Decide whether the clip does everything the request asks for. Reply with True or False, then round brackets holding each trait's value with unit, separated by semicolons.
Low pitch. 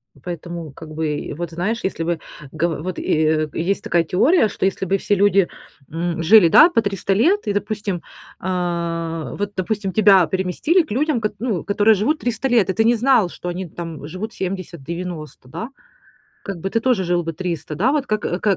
False (185 Hz)